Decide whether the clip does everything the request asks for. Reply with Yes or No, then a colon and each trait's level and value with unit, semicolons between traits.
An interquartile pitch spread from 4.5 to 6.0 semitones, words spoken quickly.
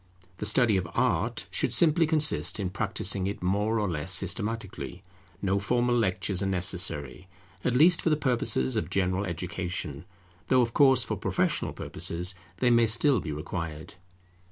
No: average, 5.1 semitones; average, 155 wpm